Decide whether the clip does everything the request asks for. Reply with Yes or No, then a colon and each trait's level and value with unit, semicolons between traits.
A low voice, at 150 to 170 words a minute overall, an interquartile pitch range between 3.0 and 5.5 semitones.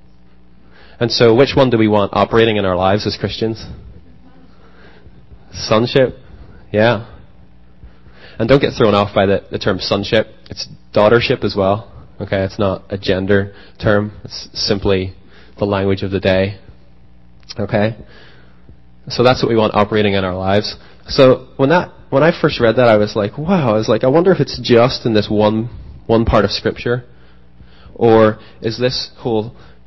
Yes: low, 100 Hz; average, 165 wpm; average, 4.3 semitones